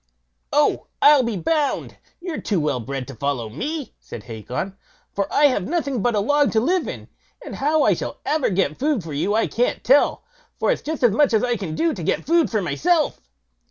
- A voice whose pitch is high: Yes, high, 240 Hz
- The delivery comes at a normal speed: No, fast, 220 wpm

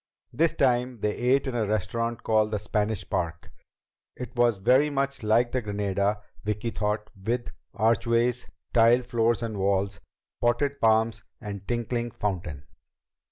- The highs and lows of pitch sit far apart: No, average, 2.7 semitones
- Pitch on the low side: Yes, low, 115 Hz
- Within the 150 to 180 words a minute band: No, average, 140 wpm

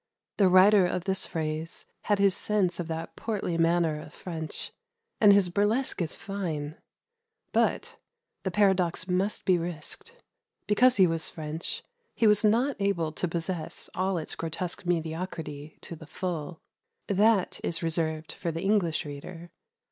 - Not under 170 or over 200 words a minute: No, average, 150 wpm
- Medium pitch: Yes, medium, 175 Hz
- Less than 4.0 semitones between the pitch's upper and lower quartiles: Yes, average, 3.5 semitones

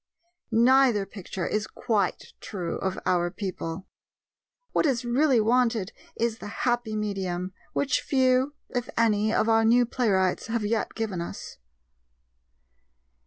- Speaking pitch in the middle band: No, high, 220 Hz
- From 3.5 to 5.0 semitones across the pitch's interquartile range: Yes, average, 4.0 semitones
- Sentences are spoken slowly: Yes, slow, 125 wpm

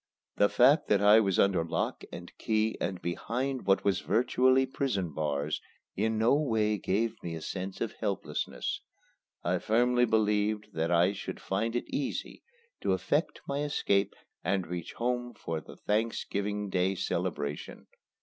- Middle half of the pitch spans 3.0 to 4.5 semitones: Yes, average, 3.8 semitones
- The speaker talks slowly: No, average, 150 wpm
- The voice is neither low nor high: No, low, 105 Hz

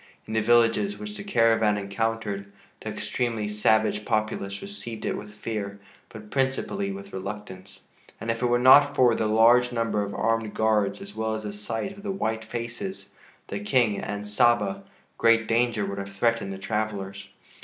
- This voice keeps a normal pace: Yes, average, 175 wpm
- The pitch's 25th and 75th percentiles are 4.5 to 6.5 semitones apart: No, narrow, 2.5 semitones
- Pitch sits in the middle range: No, low, 110 Hz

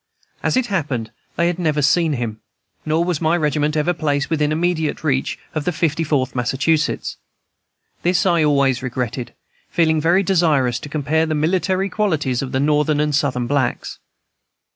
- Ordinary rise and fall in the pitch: Yes, average, 3.3 semitones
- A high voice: No, medium, 150 Hz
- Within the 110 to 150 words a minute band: No, average, 165 wpm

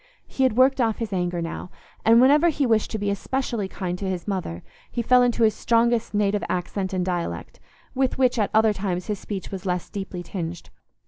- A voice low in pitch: No, high, 205 Hz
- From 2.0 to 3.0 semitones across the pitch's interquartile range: No, average, 4.4 semitones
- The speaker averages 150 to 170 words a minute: No, fast, 205 wpm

